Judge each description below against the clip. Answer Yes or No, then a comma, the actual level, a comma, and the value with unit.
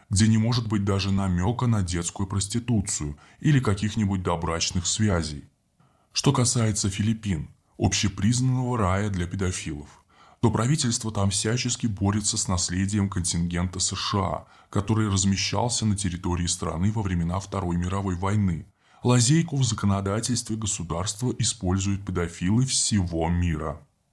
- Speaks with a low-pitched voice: Yes, low, 100 Hz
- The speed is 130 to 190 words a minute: No, average, 115 wpm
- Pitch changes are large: No, average, 3.6 semitones